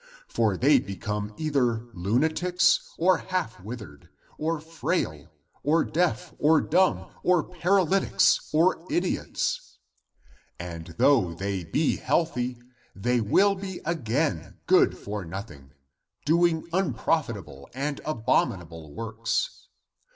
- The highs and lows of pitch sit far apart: Yes, wide, 8.5 semitones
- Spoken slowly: Yes, slow, 105 wpm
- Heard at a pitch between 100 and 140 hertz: Yes, low, 135 Hz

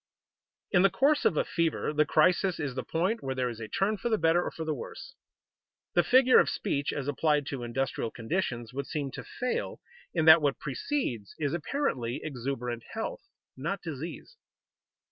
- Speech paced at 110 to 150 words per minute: No, average, 185 wpm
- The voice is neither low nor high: Yes, medium, 155 Hz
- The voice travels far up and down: Yes, wide, 6.0 semitones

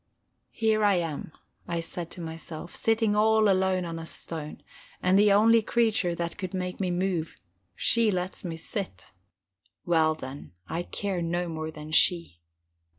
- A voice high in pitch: No, medium, 180 Hz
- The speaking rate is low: No, average, 155 wpm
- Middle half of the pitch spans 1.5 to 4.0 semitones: Yes, average, 3.7 semitones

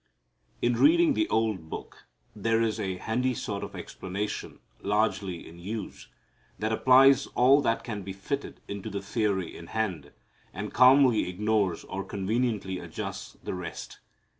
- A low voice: Yes, low, 105 Hz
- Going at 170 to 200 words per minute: No, average, 145 wpm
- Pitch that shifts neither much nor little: Yes, average, 4.0 semitones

